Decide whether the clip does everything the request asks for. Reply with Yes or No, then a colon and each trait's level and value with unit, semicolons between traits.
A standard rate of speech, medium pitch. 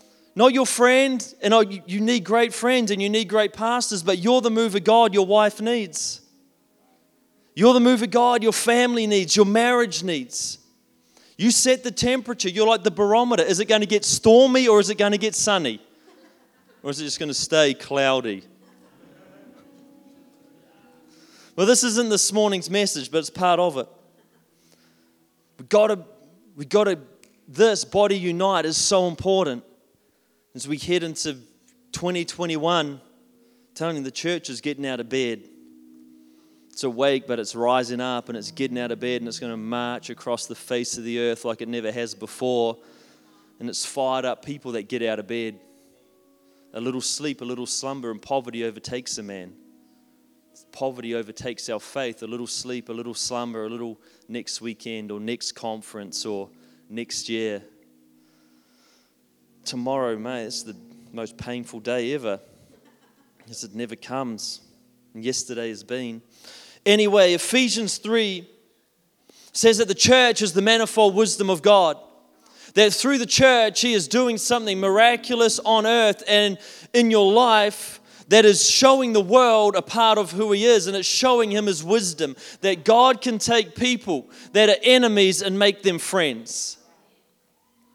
Yes: average, 165 wpm; medium, 180 Hz